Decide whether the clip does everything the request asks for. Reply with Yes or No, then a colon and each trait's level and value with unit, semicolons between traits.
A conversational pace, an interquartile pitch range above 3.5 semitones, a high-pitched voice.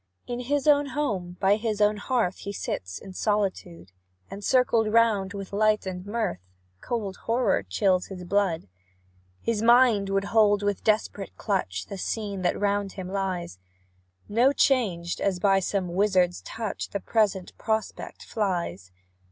No: average, 150 wpm; average, 3.1 semitones; high, 200 Hz